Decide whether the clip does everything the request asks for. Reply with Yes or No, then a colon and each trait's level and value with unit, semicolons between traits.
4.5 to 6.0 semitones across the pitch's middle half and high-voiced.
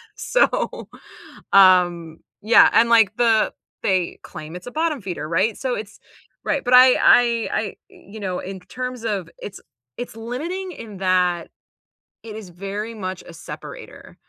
Yes: average, 4.8 semitones; high, 210 Hz